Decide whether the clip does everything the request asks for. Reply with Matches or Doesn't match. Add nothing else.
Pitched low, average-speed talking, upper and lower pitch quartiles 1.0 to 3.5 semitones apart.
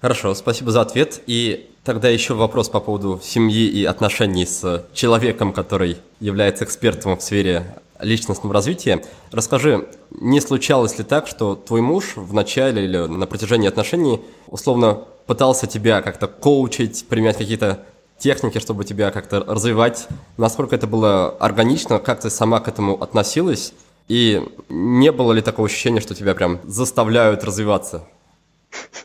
Matches